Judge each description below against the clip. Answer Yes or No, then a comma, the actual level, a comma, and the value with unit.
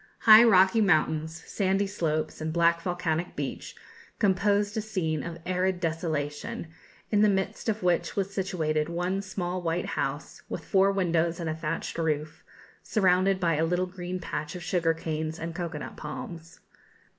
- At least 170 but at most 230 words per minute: No, average, 160 wpm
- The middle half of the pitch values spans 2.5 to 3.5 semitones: Yes, average, 2.9 semitones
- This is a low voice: No, medium, 175 Hz